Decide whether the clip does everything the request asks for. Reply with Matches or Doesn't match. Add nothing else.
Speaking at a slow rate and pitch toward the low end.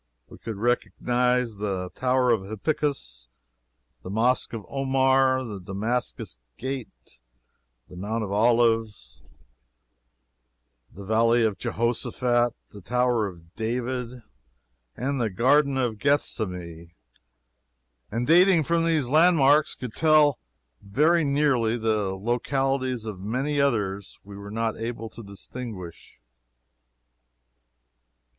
Matches